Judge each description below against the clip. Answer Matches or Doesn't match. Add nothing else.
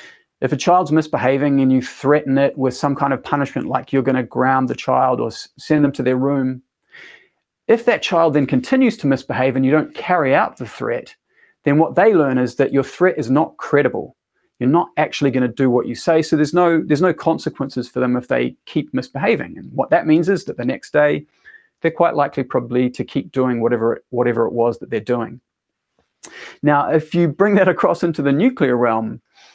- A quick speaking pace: Matches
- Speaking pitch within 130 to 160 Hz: Matches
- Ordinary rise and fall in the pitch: Matches